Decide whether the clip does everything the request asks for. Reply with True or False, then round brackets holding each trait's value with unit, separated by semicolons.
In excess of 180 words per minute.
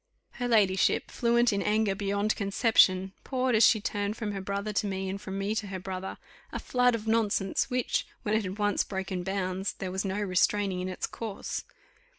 True (195 wpm)